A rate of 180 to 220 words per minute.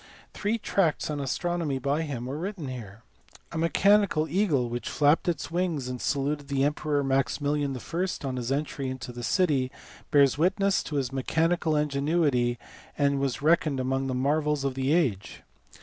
No: average, 165 wpm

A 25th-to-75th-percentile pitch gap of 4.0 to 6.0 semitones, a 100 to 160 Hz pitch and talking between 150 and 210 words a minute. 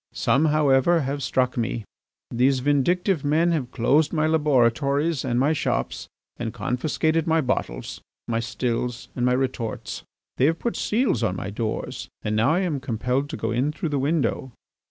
Yes: average, 4.4 semitones; low, 135 Hz; average, 170 wpm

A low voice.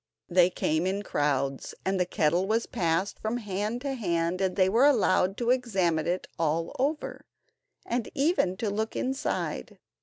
No: high, 190 Hz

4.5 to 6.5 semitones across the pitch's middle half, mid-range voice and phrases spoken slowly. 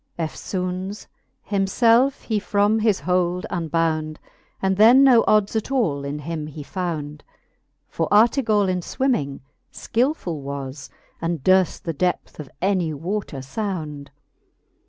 Yes: wide, 5.4 semitones; medium, 180 Hz; slow, 125 wpm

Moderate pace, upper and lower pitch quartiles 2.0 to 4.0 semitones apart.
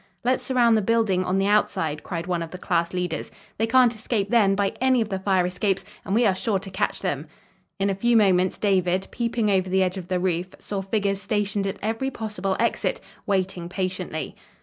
No: fast, 210 wpm; average, 2.9 semitones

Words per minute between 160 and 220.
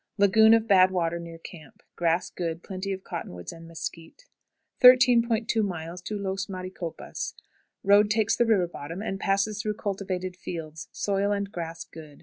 No: average, 145 wpm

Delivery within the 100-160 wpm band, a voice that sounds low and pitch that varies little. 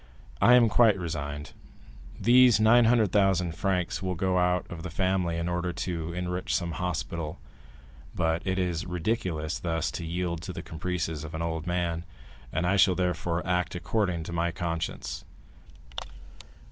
Yes: average, 150 wpm; very low, 90 Hz; narrow, 2.0 semitones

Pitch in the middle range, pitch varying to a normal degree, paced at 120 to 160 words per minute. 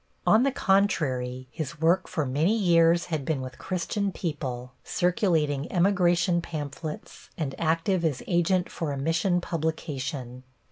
Yes: medium, 165 Hz; average, 4.0 semitones; slow, 135 wpm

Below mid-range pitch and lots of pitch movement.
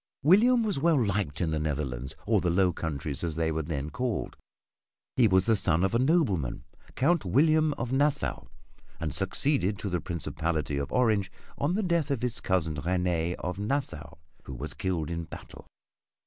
Yes: very low, 95 Hz; wide, 8.7 semitones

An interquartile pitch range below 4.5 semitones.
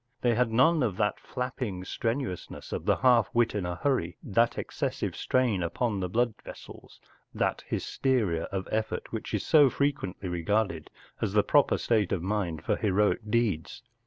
No: average, 4.9 semitones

